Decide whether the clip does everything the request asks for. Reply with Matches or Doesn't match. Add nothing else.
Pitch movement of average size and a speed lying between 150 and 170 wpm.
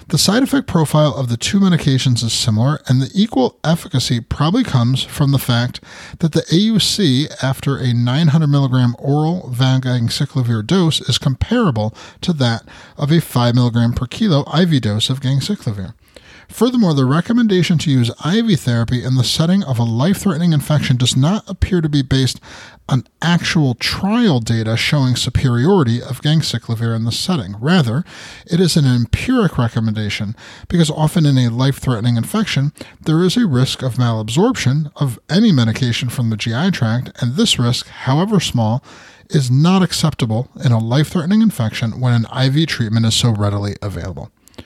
Doesn't match